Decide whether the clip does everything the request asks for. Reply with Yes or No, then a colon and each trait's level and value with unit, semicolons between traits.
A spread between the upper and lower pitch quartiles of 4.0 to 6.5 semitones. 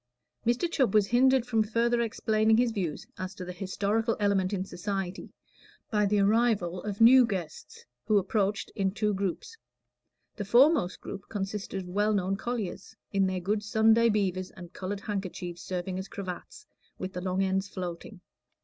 No: average, 2.9 semitones